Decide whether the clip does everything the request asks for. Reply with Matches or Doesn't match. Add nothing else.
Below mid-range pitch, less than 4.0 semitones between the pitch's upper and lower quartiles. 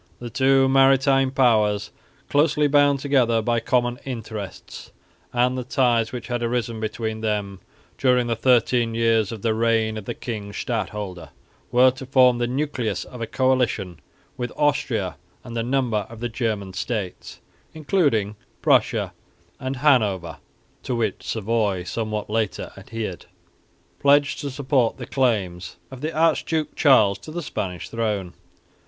Matches